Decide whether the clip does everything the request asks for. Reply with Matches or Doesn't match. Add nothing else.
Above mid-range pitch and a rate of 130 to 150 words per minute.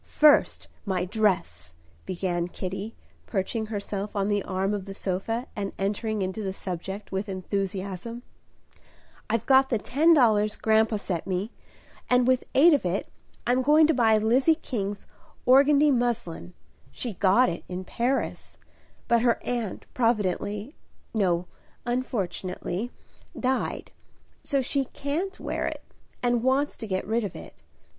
Matches